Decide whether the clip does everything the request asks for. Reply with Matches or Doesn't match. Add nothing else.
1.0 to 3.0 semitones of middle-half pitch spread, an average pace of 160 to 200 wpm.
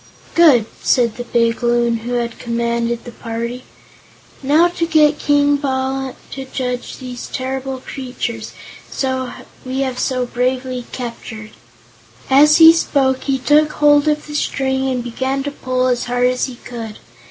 Doesn't match